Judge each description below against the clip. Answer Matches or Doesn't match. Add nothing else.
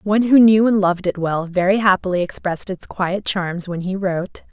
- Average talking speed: Doesn't match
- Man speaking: Doesn't match